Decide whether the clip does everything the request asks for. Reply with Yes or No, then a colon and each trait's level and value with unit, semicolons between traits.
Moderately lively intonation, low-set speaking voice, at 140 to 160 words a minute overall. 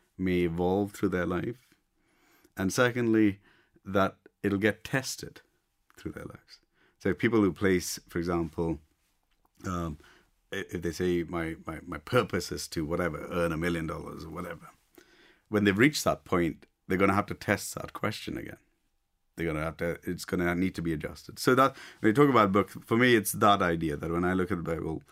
No: average, 3.0 semitones; very low, 90 Hz; average, 200 wpm